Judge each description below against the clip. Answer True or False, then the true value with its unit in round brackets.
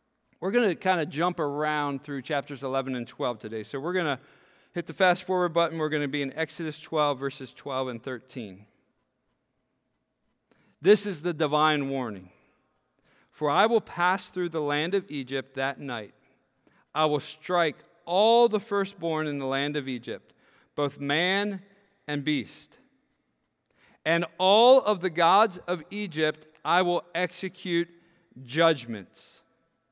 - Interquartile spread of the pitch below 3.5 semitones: False (4.2 semitones)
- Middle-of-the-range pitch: True (155 Hz)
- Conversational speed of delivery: True (150 wpm)